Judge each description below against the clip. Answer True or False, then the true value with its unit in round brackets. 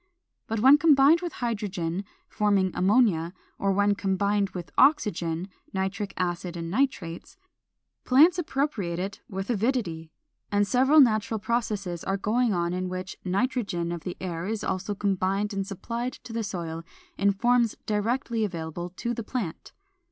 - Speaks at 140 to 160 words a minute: True (145 wpm)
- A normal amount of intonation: True (4.6 semitones)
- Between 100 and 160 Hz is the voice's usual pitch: False (200 Hz)